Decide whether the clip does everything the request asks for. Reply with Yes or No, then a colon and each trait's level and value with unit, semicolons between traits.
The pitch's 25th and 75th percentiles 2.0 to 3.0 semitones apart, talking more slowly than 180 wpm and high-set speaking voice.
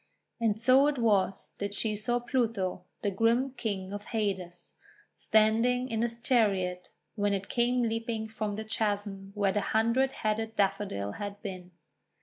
Yes: average, 2.7 semitones; average, 150 wpm; high, 215 Hz